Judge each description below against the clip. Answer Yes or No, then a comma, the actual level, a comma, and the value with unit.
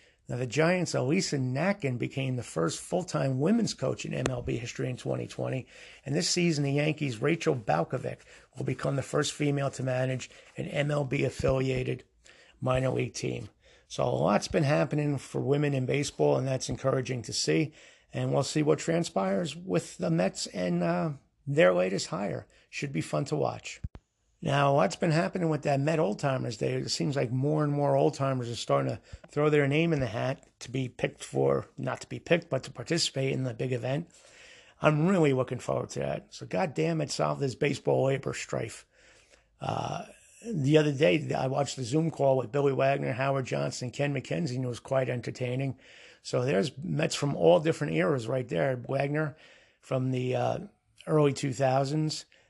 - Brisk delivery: No, average, 185 wpm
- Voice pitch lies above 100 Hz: Yes, medium, 140 Hz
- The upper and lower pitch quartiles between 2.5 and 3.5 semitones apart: Yes, average, 3.2 semitones